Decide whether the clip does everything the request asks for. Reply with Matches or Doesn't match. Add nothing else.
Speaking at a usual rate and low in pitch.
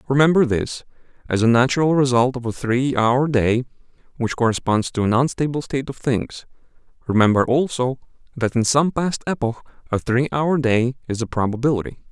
Matches